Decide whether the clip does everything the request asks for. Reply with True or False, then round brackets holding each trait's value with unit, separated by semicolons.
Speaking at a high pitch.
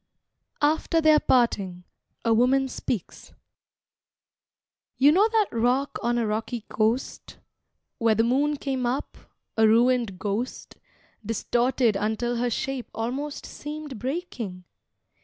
True (245 Hz)